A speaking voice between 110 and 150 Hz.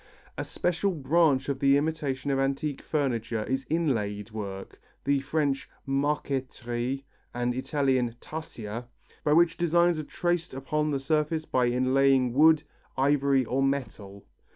Yes: low, 135 Hz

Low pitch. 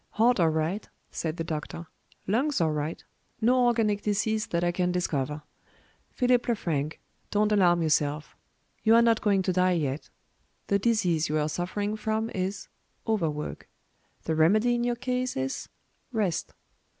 No: high, 190 Hz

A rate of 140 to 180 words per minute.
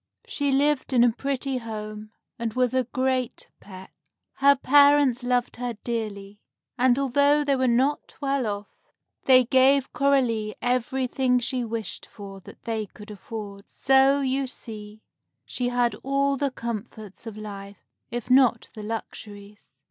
Yes: average, 145 wpm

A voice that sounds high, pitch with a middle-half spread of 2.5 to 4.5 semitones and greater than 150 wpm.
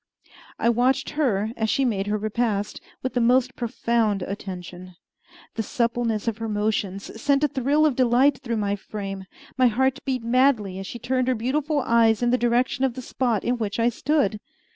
Yes: high, 235 Hz; average, 3.4 semitones; average, 185 wpm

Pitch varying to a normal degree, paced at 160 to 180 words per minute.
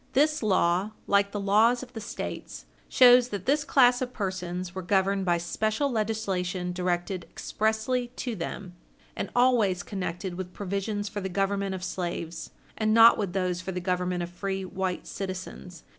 Yes: average, 3.3 semitones; average, 165 wpm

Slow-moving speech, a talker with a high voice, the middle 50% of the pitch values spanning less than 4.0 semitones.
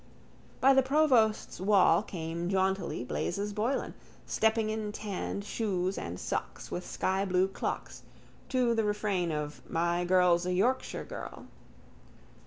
Yes: slow, 125 wpm; high, 195 Hz; average, 3.5 semitones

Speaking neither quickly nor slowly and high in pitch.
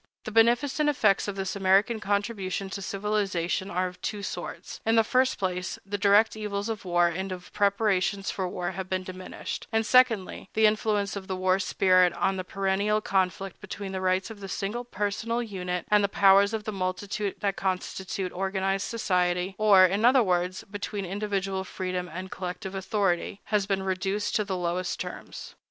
Yes: average, 175 wpm; high, 195 Hz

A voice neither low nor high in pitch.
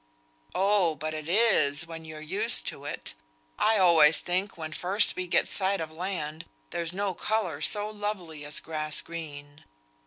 Yes: medium, 165 Hz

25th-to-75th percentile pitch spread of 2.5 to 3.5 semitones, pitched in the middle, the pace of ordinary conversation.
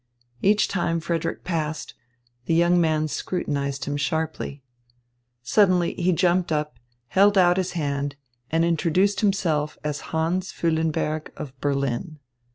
No: average, 3.1 semitones; medium, 165 Hz; slow, 125 wpm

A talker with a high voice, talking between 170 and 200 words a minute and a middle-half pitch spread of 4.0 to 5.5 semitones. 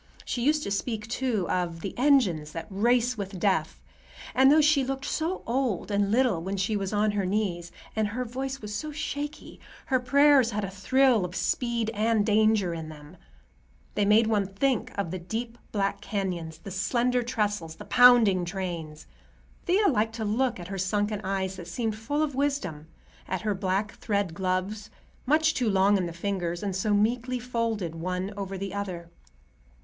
Yes: high, 205 Hz; average, 180 wpm; average, 4.6 semitones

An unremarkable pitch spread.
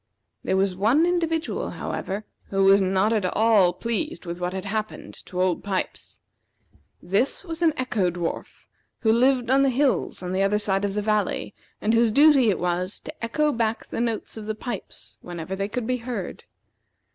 Yes: average, 4.7 semitones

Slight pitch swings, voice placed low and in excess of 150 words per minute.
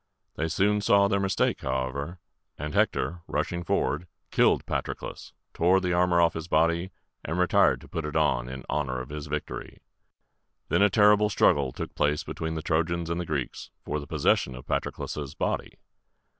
No: average, 3.6 semitones; very low, 80 Hz; average, 170 wpm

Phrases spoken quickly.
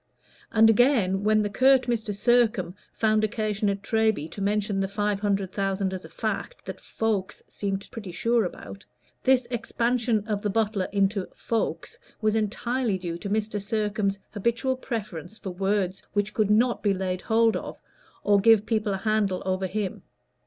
No: average, 165 wpm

